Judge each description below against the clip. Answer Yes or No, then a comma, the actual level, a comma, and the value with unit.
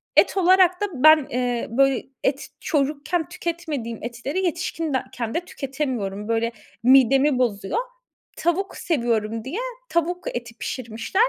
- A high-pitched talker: Yes, very high, 275 Hz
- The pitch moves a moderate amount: No, wide, 6.1 semitones